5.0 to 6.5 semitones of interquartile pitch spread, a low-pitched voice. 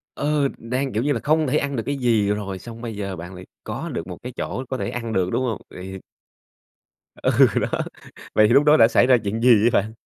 No: average, 4.3 semitones; low, 115 Hz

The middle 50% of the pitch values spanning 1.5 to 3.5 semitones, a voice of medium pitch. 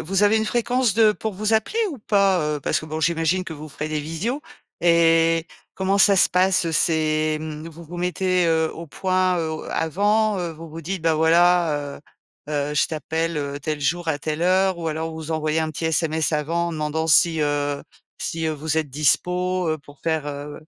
Yes: average, 2.9 semitones; medium, 165 Hz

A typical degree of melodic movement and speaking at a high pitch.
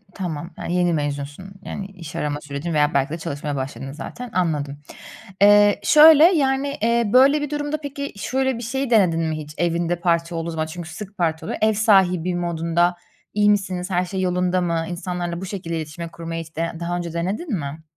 No: average, 4.1 semitones; medium, 175 Hz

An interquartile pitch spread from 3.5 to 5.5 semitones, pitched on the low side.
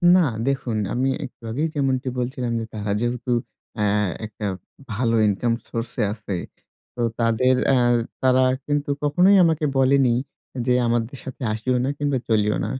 No: average, 2.9 semitones; low, 125 Hz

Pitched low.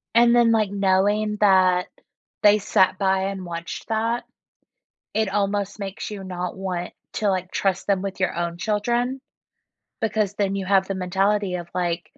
No: high, 195 Hz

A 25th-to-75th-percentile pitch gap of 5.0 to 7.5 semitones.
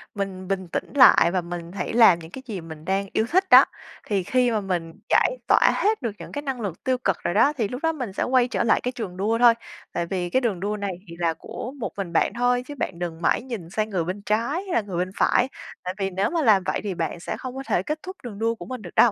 Yes: wide, 5.5 semitones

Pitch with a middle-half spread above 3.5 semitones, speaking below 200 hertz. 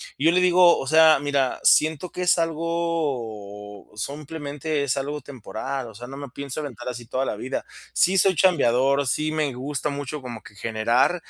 Yes: average, 4.2 semitones; medium, 140 Hz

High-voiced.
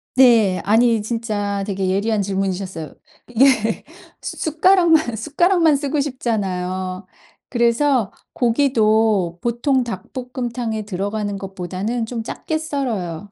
Yes: high, 225 Hz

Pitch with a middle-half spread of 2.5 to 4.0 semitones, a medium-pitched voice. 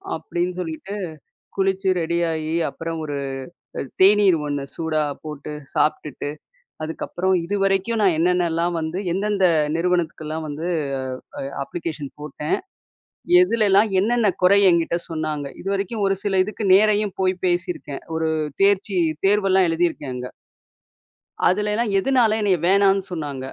Yes: average, 3.7 semitones; medium, 180 Hz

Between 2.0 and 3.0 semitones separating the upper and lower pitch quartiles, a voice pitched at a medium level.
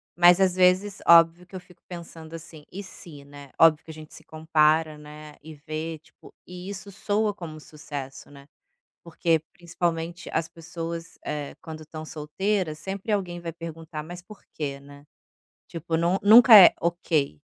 Yes: narrow, 2.6 semitones; medium, 165 Hz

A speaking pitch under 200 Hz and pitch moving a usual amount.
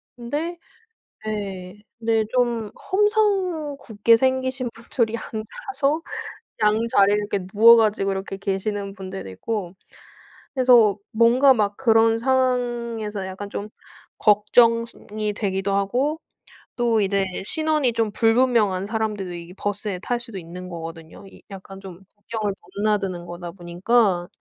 No: high, 215 Hz; average, 3.7 semitones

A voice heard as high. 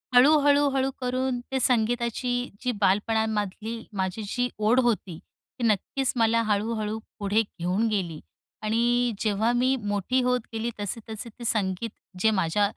Yes: high, 225 Hz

